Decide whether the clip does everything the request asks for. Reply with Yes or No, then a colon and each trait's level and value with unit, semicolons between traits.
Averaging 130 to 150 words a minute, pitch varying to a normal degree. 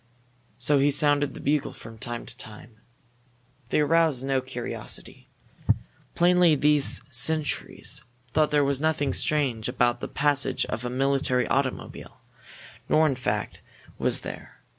Yes: slow, 135 wpm; average, 3.1 semitones